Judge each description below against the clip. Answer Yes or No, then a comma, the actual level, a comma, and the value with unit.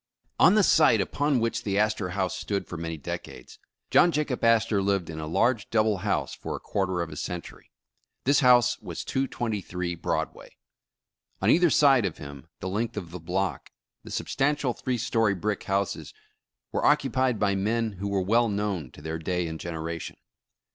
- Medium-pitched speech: No, low, 100 Hz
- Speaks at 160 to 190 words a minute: Yes, average, 175 wpm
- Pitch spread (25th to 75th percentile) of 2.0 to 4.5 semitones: No, average, 5.2 semitones